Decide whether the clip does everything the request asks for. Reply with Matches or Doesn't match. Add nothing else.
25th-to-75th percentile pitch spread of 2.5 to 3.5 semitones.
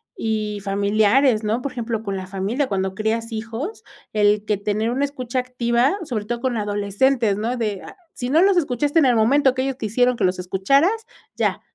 Doesn't match